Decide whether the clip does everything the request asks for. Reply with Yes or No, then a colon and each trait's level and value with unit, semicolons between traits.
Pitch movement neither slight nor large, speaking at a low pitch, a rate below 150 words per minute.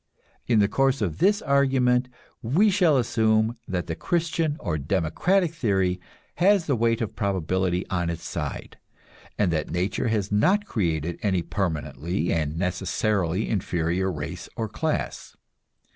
No: wide, 7.0 semitones; low, 100 Hz; average, 140 wpm